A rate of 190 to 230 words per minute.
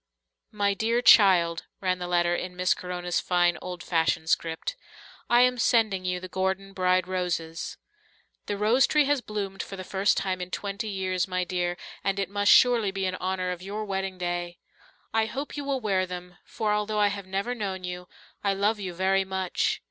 Yes: average, 195 wpm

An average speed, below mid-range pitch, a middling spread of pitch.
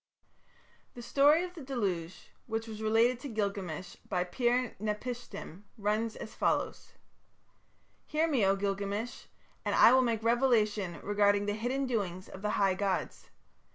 No: average, 145 wpm; high, 215 Hz; average, 3.6 semitones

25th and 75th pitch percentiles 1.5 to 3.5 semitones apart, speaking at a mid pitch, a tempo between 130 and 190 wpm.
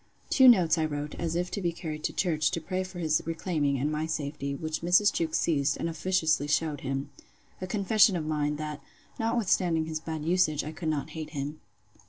No: average, 2.7 semitones; medium, 160 Hz; fast, 205 wpm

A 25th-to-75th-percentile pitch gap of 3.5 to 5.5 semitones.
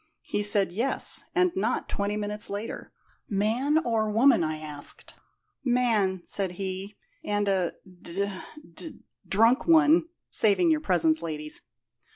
Yes: average, 4.6 semitones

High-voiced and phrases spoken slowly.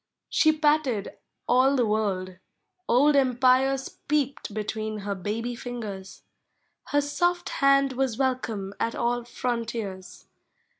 Yes: high, 245 Hz; slow, 110 wpm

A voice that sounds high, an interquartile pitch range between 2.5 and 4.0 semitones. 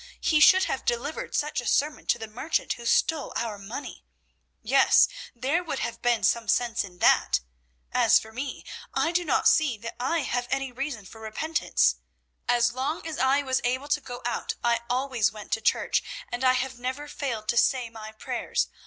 Yes: very high, 250 Hz; average, 3.7 semitones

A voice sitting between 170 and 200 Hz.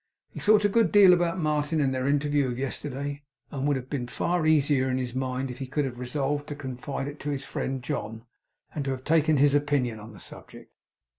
No: medium, 140 Hz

